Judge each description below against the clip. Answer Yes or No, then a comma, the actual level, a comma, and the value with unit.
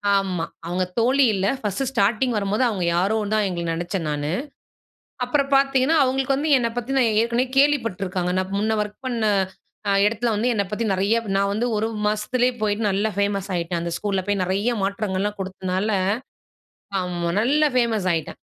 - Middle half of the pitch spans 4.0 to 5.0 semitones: Yes, average, 4.3 semitones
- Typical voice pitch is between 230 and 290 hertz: No, high, 210 Hz